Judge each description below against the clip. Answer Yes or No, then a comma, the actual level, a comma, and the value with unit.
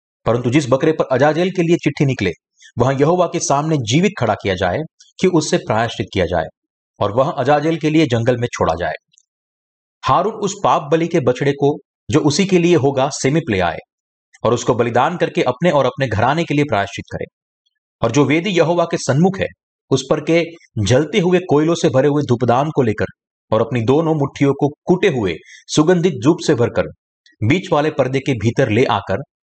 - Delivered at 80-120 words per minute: No, fast, 190 wpm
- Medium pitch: Yes, medium, 145 Hz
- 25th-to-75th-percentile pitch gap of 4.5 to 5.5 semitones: Yes, average, 5.1 semitones